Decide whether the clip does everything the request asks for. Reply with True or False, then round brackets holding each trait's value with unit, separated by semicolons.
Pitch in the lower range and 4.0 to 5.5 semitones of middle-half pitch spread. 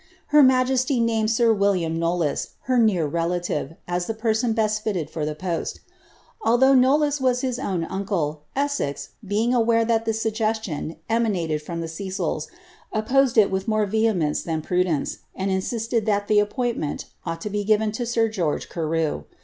False (215 Hz; 5.1 semitones)